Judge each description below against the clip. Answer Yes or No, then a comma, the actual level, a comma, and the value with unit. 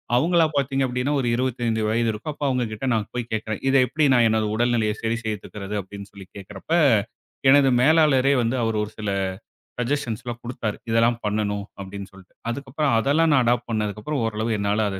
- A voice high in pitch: No, low, 115 Hz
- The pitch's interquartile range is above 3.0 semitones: Yes, average, 3.7 semitones